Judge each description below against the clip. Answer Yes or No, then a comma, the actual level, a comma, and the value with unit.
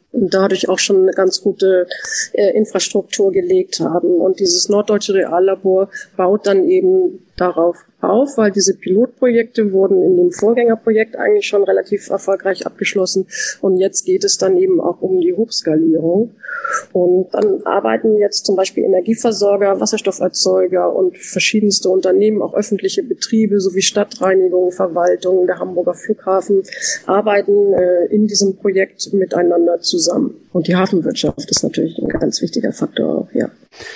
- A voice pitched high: Yes, high, 200 Hz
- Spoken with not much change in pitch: No, average, 3.4 semitones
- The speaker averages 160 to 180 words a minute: No, average, 145 wpm